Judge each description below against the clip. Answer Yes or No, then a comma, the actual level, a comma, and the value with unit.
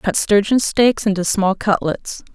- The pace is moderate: Yes, average, 155 wpm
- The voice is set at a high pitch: Yes, high, 205 Hz